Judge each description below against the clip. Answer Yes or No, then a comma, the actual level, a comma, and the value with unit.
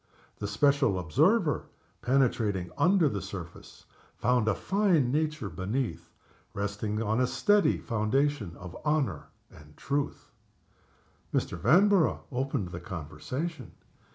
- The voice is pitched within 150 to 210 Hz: No, low, 120 Hz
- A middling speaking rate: No, slow, 110 wpm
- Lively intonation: Yes, wide, 6.7 semitones